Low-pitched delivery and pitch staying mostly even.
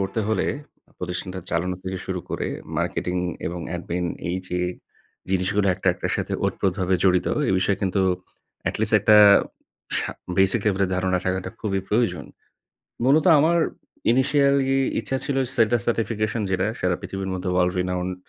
No: very low, 95 Hz; average, 3.2 semitones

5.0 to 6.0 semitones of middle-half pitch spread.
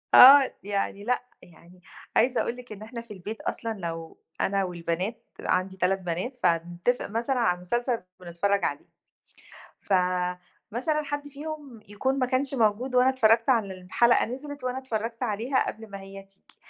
Yes: wide, 5.5 semitones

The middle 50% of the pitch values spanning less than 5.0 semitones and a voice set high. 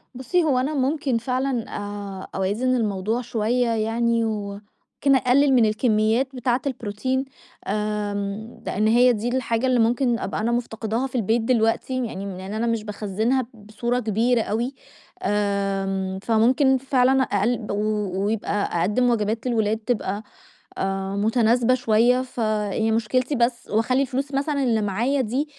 Yes: average, 3.3 semitones; high, 230 Hz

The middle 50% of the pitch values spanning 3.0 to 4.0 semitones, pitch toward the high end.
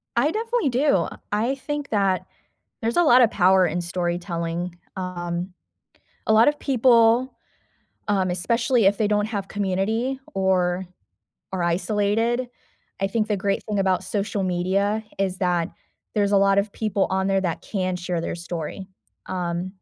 Yes: average, 3.6 semitones; high, 195 Hz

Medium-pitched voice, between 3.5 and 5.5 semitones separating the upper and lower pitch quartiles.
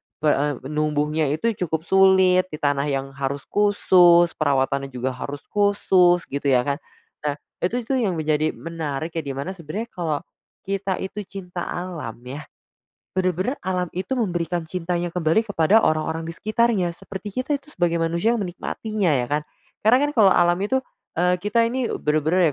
Yes: medium, 175 Hz; average, 4.3 semitones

